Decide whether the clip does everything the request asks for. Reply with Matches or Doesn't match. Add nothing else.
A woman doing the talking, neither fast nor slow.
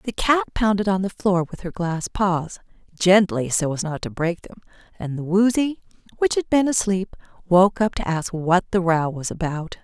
Matches